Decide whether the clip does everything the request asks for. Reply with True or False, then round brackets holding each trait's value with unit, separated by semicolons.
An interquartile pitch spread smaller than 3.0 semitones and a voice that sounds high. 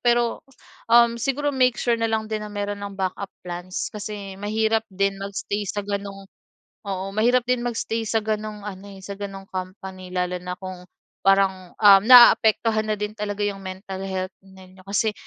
True (2.4 semitones; 200 Hz)